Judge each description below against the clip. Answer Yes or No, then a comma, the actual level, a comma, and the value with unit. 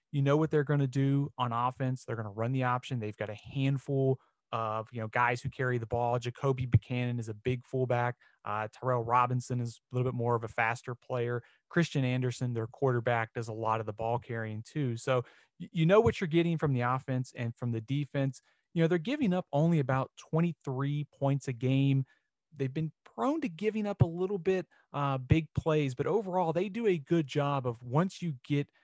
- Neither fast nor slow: No, fast, 215 wpm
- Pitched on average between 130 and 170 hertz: Yes, low, 135 Hz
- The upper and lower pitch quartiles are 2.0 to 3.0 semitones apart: No, average, 3.8 semitones